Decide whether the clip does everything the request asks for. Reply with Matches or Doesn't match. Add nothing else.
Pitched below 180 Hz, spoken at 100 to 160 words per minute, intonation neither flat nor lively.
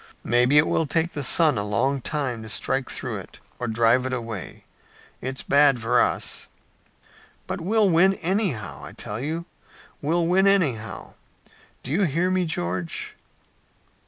Doesn't match